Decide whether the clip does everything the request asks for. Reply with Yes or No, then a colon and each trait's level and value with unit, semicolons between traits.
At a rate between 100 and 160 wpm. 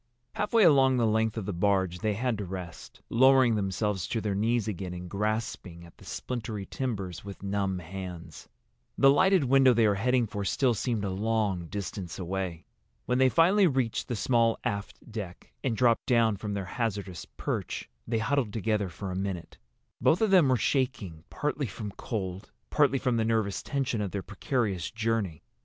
No: average, 180 wpm